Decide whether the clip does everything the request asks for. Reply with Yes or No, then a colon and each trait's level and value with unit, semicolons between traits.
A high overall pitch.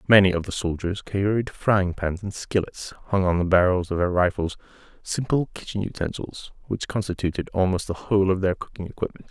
No: very low, 95 Hz